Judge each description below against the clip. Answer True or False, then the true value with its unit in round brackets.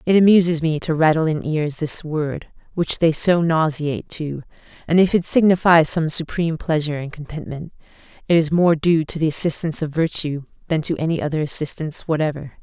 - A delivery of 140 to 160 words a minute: False (180 wpm)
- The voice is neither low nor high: True (160 Hz)